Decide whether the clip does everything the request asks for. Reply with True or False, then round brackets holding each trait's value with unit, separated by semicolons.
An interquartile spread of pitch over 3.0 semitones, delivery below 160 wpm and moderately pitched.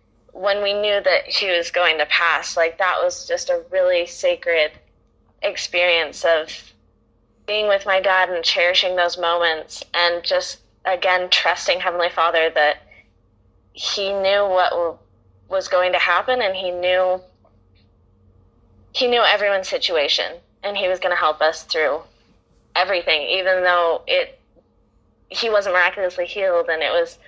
True (3.9 semitones; 145 wpm; 180 Hz)